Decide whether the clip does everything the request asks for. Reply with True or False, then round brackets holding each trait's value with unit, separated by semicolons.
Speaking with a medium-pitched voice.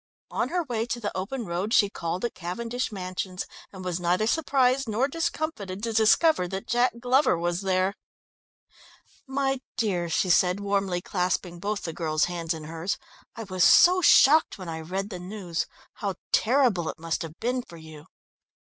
False (195 Hz)